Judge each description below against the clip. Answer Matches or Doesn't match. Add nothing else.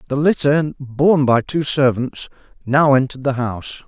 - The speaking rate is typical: Matches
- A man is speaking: Matches